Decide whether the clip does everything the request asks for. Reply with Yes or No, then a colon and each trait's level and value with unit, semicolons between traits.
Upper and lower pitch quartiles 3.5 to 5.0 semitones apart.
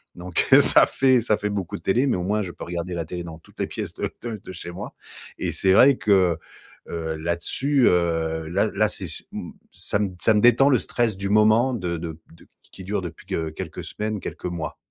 Yes: average, 4.1 semitones